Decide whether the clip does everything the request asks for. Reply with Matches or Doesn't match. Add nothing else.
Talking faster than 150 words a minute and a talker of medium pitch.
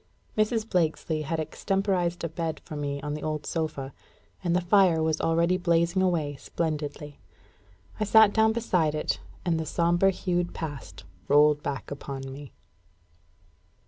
Doesn't match